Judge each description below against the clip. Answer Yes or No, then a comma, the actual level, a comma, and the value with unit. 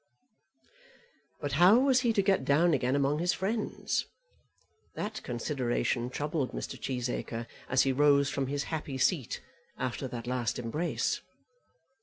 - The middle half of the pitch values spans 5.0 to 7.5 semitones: Yes, average, 5.3 semitones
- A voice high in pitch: No, medium, 140 Hz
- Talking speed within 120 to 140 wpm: Yes, slow, 135 wpm